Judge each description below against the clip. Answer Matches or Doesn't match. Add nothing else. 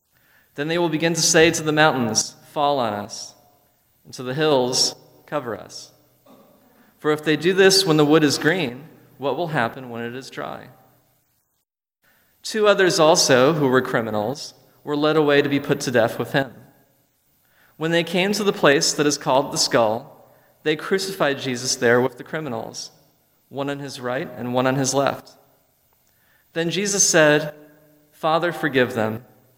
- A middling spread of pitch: Matches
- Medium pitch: Matches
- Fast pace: Doesn't match